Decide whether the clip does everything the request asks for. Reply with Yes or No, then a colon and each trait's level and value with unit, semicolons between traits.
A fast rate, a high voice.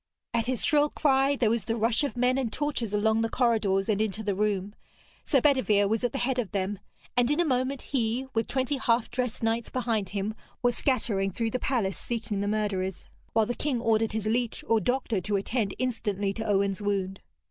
Yes: fast, 210 wpm; high, 225 Hz